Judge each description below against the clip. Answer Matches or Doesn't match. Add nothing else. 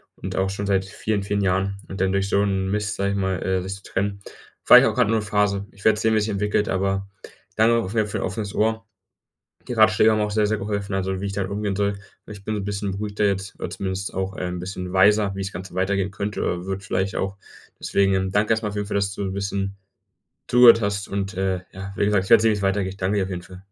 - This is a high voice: Doesn't match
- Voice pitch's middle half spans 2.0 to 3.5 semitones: Doesn't match